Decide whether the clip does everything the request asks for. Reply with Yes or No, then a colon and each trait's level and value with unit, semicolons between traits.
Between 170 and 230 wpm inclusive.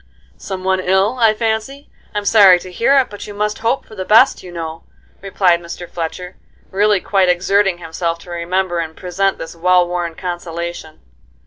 Yes: average, 180 wpm